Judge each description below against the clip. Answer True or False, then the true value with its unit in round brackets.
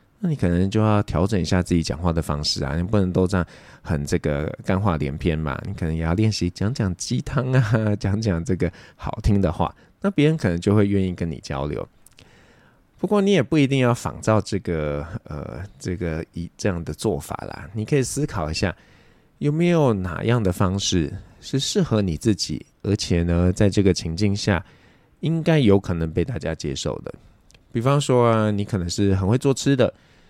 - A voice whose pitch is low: True (100 Hz)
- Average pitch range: True (4.7 semitones)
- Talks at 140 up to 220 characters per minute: False (280 characters per minute)